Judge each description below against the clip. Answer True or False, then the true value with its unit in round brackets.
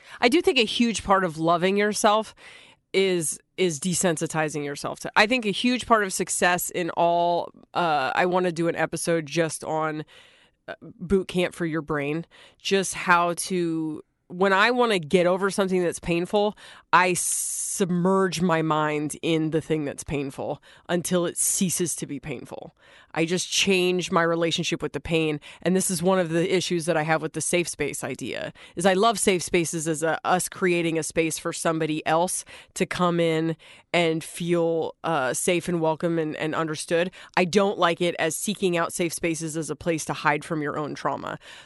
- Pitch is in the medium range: True (170 Hz)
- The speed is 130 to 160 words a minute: False (190 wpm)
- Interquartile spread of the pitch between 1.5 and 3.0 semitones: True (2.6 semitones)